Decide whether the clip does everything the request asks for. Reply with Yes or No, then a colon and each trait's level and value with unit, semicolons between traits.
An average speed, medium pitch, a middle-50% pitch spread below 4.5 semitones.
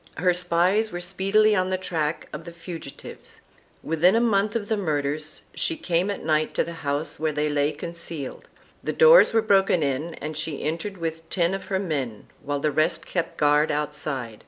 Yes: average, 190 wpm; medium, 165 Hz; average, 3.9 semitones